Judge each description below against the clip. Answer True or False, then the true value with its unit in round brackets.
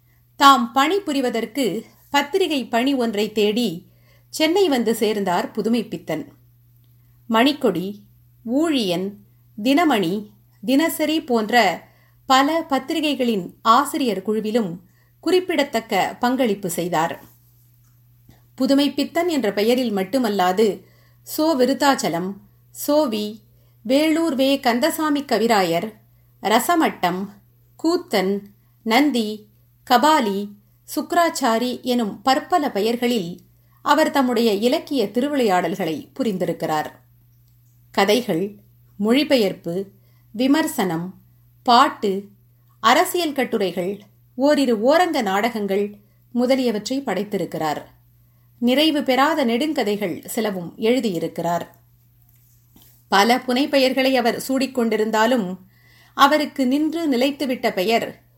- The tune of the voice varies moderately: False (8.6 semitones)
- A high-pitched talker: True (220 Hz)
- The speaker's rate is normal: False (70 wpm)